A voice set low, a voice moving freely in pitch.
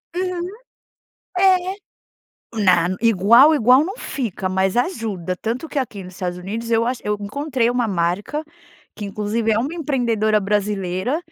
No: high, 225 Hz; wide, 5.7 semitones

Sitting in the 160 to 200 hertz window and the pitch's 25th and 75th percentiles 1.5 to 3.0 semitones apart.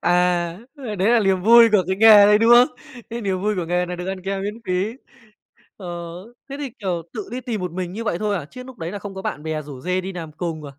No: high, 195 Hz; average, 3.7 semitones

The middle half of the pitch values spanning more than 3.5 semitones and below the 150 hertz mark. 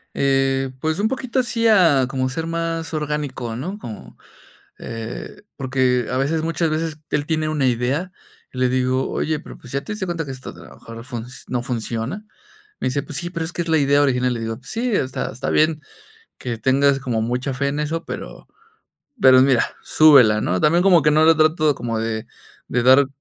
Yes: average, 4.3 semitones; medium, 140 Hz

